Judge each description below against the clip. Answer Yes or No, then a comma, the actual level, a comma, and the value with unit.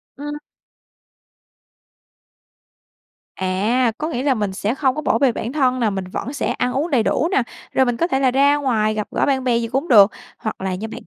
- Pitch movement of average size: Yes, average, 4.2 semitones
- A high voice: Yes, very high, 250 Hz